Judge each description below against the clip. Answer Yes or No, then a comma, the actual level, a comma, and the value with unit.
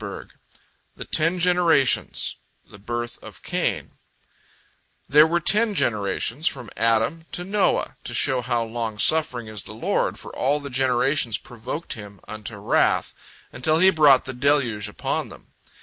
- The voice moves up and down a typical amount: No, wide, 5.8 semitones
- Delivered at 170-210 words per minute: No, average, 150 wpm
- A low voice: Yes, low, 130 Hz